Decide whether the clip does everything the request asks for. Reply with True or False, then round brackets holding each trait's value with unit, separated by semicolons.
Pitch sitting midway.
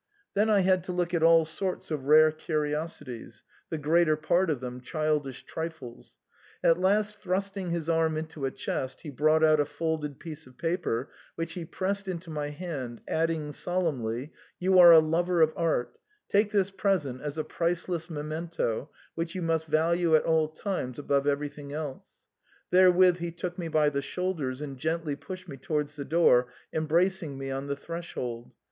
True (160 Hz)